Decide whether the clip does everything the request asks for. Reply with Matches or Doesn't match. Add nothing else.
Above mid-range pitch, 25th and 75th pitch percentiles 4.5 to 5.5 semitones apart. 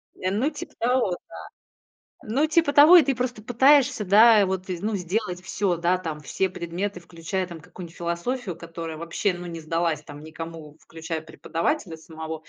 Doesn't match